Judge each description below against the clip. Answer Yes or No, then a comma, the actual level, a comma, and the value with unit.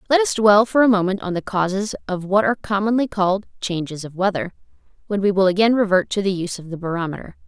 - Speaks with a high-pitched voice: Yes, high, 195 Hz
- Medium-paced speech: No, fast, 225 wpm